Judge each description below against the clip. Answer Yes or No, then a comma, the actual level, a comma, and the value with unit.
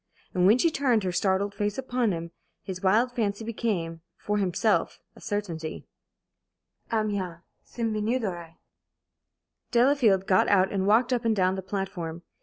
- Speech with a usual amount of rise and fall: Yes, average, 3.6 semitones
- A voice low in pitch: No, high, 205 Hz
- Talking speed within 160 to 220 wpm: No, average, 150 wpm